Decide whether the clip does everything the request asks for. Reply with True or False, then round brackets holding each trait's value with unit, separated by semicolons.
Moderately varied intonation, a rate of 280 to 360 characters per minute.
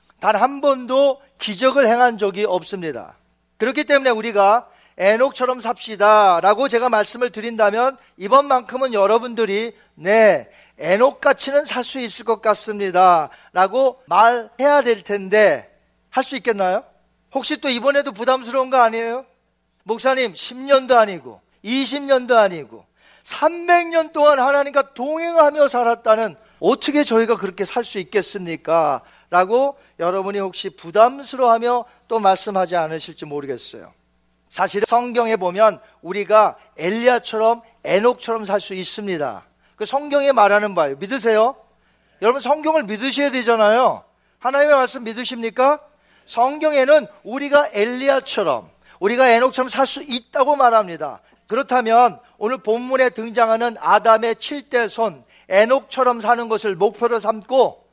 True (4.4 semitones; 305 characters per minute)